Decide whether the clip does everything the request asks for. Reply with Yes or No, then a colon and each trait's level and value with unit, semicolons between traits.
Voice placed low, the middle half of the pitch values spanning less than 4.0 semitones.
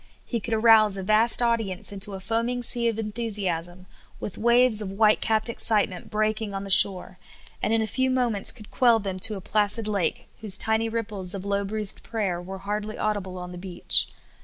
No: high, 210 Hz; average, 2.7 semitones